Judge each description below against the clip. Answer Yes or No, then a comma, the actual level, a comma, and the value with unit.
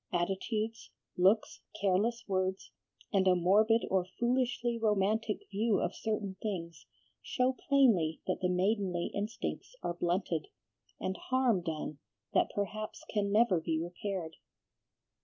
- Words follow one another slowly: Yes, slow, 120 wpm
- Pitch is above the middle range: Yes, high, 200 Hz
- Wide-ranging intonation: No, average, 3.6 semitones